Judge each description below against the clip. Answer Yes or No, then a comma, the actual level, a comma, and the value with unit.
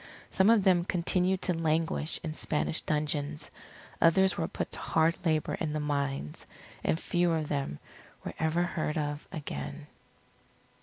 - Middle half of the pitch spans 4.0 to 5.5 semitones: No, average, 2.7 semitones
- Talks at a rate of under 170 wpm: Yes, average, 150 wpm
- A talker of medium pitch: Yes, medium, 160 Hz